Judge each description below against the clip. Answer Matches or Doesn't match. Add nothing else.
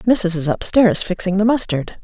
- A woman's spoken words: Matches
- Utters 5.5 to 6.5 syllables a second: Doesn't match